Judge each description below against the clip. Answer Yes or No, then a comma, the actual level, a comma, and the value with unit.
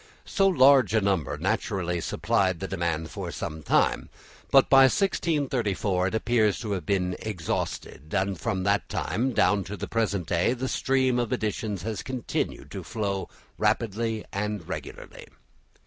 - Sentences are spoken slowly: No, average, 150 wpm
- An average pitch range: Yes, average, 4.6 semitones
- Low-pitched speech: Yes, low, 105 Hz